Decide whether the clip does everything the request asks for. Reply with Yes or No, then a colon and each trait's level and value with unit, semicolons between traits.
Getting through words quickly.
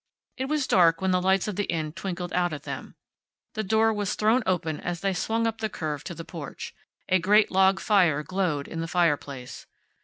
Yes: fast, 210 wpm